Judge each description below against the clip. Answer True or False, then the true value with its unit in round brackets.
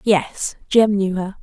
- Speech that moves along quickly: False (170 wpm)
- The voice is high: True (200 Hz)